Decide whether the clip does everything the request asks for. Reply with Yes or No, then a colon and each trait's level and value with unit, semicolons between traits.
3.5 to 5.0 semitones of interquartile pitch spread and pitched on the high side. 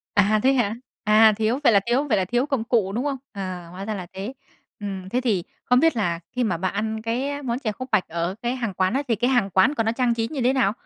Yes: average, 4.3 semitones; high, 225 Hz